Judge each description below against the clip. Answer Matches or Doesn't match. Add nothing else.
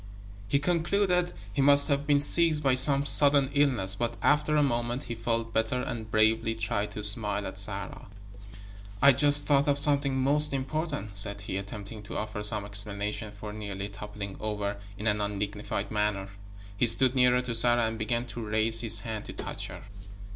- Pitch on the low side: Matches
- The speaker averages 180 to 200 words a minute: Matches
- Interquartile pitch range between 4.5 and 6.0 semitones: Matches